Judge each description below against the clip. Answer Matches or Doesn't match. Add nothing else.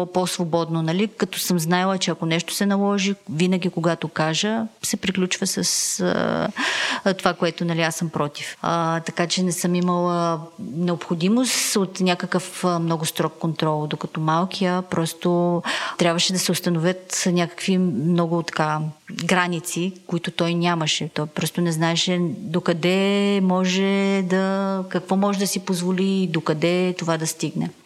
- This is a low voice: Doesn't match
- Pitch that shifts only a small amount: Matches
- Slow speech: Doesn't match